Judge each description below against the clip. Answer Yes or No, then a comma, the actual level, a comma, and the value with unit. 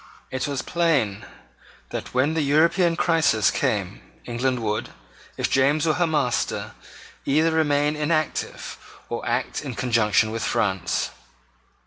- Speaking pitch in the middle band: Yes, medium, 145 Hz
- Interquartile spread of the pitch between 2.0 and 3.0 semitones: No, average, 5.2 semitones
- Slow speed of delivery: Yes, slow, 125 wpm